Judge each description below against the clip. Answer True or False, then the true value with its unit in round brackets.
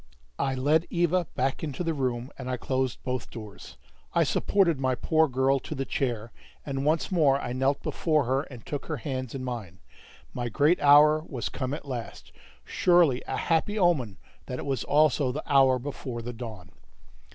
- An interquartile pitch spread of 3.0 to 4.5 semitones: True (3.4 semitones)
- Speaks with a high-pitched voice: False (135 Hz)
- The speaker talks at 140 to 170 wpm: False (185 wpm)